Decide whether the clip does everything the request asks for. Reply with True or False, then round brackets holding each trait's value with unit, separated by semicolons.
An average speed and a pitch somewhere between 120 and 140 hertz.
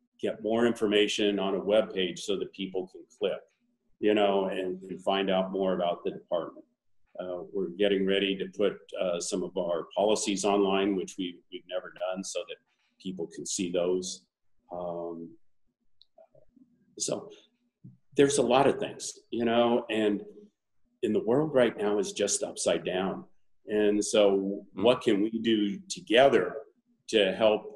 False (160 wpm; 105 Hz)